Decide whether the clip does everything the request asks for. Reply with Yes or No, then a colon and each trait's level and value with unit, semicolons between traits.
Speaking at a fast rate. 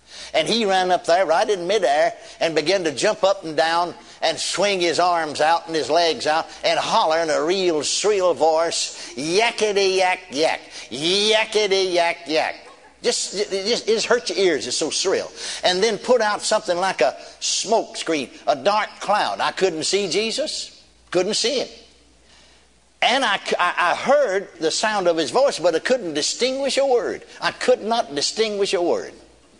No: average, 180 wpm